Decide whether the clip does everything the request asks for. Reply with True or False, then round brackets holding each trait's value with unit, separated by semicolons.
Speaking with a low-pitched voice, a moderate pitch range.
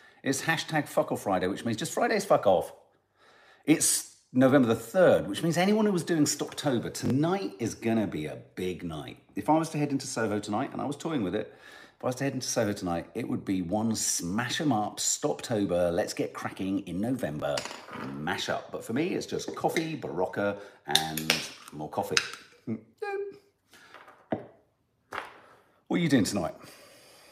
False (115 Hz; 7.9 semitones)